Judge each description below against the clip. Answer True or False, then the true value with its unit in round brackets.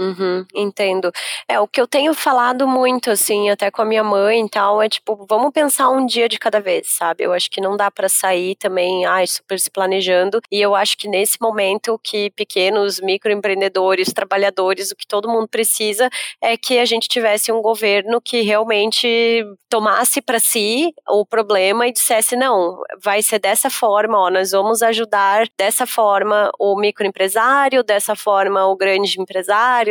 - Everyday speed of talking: True (175 wpm)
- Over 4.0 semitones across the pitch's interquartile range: False (2.7 semitones)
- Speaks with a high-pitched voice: True (210 Hz)